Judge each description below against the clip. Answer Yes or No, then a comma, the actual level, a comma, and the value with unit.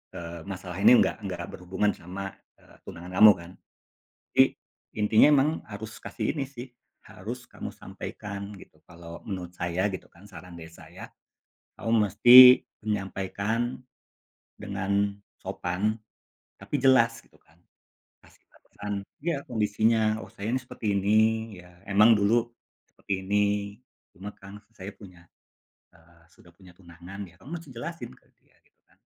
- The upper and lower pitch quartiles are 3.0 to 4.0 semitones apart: Yes, average, 3.5 semitones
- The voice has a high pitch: No, low, 100 Hz